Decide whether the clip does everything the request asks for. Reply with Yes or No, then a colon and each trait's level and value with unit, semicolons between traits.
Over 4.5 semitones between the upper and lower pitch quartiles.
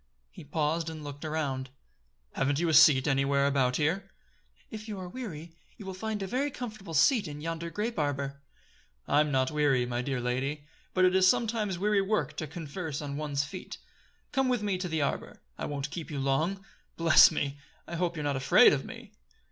Yes: average, 5.2 semitones